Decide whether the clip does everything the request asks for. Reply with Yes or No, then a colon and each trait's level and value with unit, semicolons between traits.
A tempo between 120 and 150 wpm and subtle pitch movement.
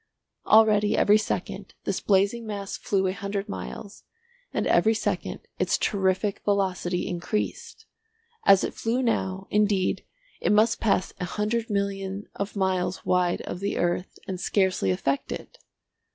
Yes: average, 140 wpm; narrow, 2.0 semitones